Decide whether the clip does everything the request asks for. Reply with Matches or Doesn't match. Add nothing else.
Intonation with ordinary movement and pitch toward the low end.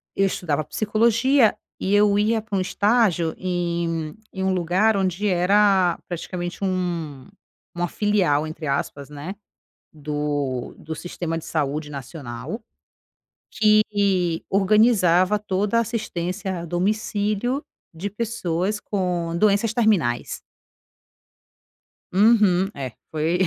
Doesn't match